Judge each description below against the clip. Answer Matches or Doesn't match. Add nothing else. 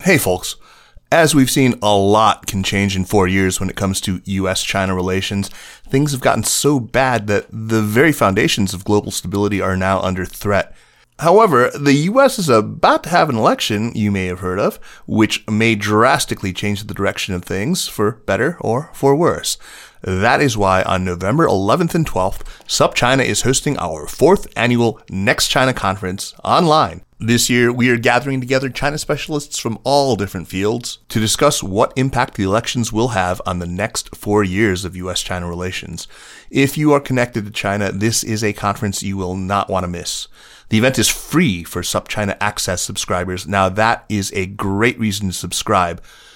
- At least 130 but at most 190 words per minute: Matches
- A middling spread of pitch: Matches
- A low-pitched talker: Matches